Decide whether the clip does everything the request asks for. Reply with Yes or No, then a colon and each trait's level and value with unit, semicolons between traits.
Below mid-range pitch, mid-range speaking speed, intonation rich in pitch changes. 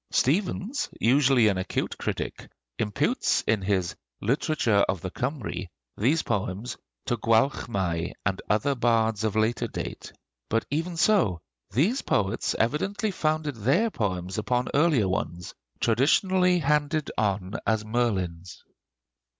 No: low, 115 Hz; slow, 120 wpm; wide, 7.1 semitones